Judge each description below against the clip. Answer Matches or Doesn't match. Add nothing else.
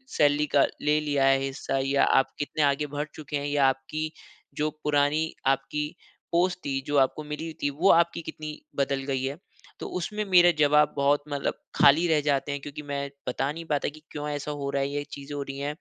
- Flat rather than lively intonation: Matches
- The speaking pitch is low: Doesn't match